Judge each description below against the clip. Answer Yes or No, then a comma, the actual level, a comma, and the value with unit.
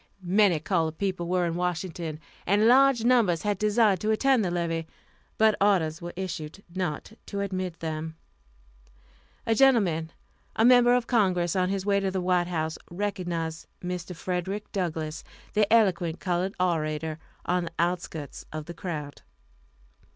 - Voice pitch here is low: No, medium, 180 Hz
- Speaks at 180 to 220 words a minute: No, average, 150 wpm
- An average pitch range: Yes, average, 3.6 semitones